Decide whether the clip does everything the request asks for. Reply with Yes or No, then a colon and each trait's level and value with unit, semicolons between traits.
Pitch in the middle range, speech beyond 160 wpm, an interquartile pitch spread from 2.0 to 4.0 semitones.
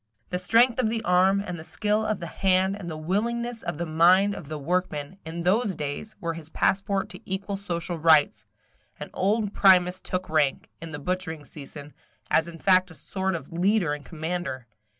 Yes: medium, 180 Hz; average, 190 wpm; average, 3.5 semitones